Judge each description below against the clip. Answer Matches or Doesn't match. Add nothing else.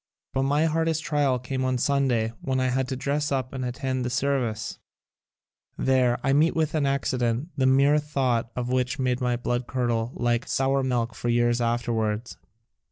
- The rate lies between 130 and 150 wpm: Doesn't match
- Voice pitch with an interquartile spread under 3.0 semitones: Matches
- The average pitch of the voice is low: Matches